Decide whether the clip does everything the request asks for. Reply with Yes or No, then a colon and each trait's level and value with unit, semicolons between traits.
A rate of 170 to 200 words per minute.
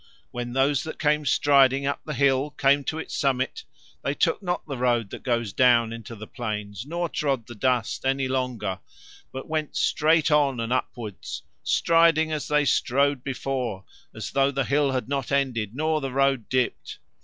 Yes: average, 180 wpm